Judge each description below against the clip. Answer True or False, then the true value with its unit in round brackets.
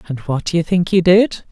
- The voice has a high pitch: False (170 Hz)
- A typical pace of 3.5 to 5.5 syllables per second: True (5.3 syllables/s)